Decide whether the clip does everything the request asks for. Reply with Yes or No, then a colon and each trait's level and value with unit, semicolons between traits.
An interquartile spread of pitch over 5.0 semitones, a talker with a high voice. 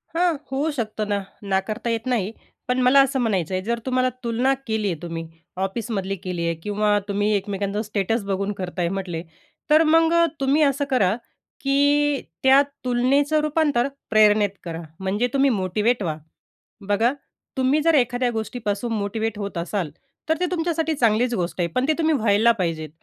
Yes: wide, 5.4 semitones; high, 225 Hz